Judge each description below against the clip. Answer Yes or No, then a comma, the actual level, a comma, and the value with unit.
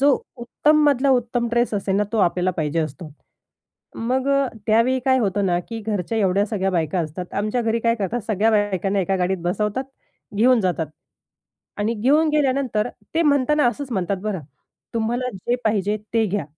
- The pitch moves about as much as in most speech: Yes, average, 4.6 semitones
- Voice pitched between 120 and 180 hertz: No, high, 220 Hz